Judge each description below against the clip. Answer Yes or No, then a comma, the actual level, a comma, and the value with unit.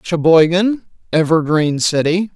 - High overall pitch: No, medium, 170 Hz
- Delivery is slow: Yes, slow, 75 wpm